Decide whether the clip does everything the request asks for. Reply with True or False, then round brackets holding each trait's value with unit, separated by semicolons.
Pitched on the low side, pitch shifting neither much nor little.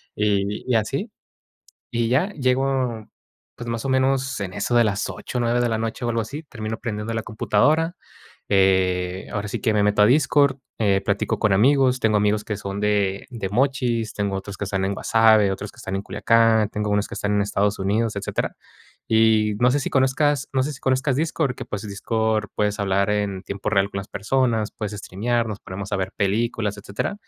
True (110 Hz; 3.5 semitones)